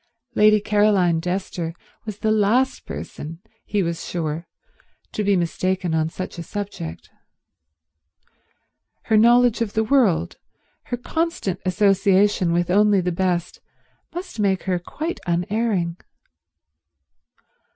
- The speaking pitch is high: Yes, high, 195 Hz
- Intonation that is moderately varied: Yes, average, 3.7 semitones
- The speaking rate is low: Yes, slow, 115 wpm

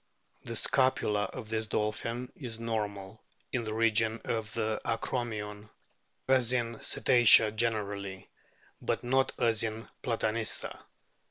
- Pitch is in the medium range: No, low, 110 Hz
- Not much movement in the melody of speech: Yes, narrow, 1.7 semitones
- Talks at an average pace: No, slow, 115 wpm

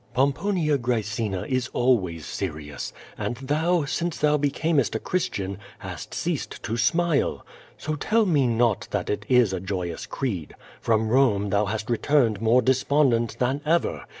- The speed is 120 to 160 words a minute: Yes, average, 150 wpm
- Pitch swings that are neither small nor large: No, wide, 5.7 semitones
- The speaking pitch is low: Yes, low, 125 Hz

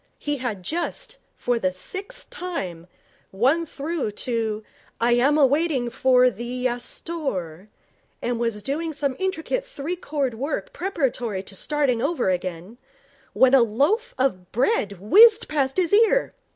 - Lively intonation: Yes, wide, 6.6 semitones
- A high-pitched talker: Yes, very high, 265 Hz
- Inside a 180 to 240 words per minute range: No, average, 145 wpm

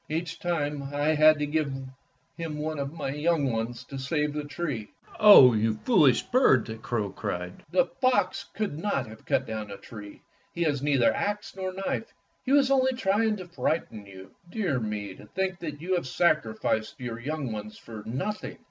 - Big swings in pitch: Yes, wide, 7.4 semitones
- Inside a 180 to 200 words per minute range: Yes, average, 185 wpm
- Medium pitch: Yes, medium, 150 Hz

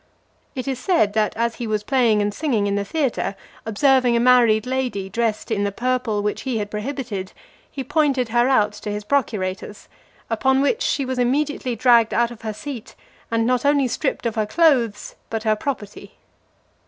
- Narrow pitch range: No, average, 3.7 semitones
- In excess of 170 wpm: Yes, average, 185 wpm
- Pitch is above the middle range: Yes, high, 235 Hz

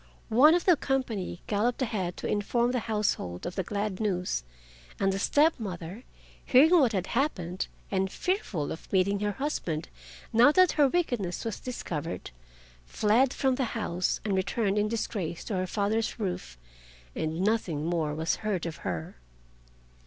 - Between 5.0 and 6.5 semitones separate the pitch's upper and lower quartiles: Yes, average, 5.3 semitones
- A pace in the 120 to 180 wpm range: Yes, average, 160 wpm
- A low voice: No, high, 205 Hz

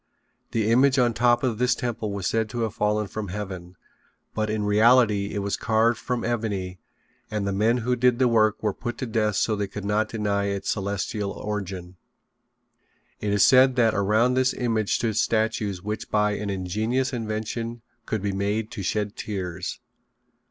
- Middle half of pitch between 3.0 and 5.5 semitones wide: No, narrow, 2.5 semitones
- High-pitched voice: No, low, 110 Hz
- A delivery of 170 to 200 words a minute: Yes, average, 180 wpm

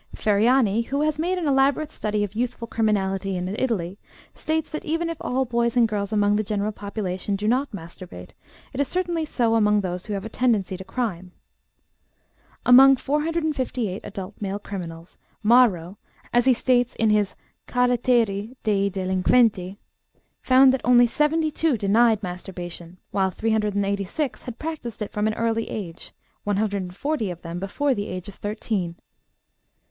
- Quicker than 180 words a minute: No, average, 155 wpm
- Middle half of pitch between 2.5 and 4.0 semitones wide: No, average, 4.5 semitones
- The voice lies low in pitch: No, high, 215 Hz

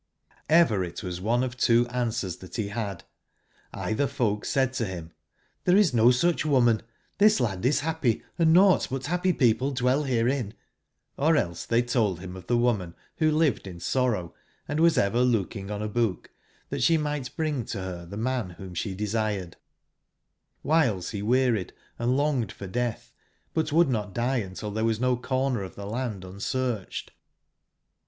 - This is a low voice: Yes, low, 120 Hz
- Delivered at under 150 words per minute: No, average, 170 wpm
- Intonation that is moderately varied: Yes, average, 5.0 semitones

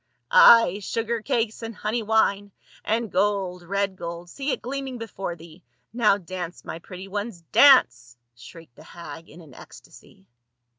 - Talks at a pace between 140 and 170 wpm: Yes, average, 160 wpm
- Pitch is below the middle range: No, high, 195 Hz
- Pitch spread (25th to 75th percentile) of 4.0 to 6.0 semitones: Yes, average, 5.0 semitones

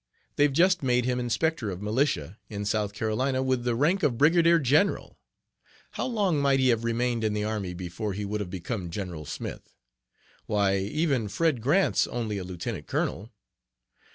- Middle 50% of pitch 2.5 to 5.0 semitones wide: No, wide, 5.5 semitones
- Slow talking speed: No, average, 170 wpm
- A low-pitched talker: Yes, low, 115 Hz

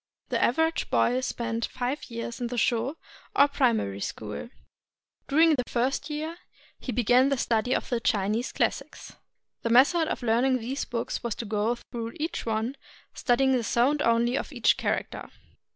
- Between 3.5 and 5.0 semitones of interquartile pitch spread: No, average, 2.8 semitones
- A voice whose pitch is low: No, high, 245 Hz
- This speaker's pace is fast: No, average, 165 wpm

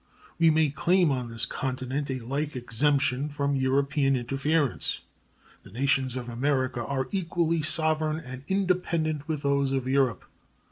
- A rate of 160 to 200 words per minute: No, average, 140 wpm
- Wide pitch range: No, average, 3.1 semitones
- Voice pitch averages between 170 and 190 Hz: No, medium, 140 Hz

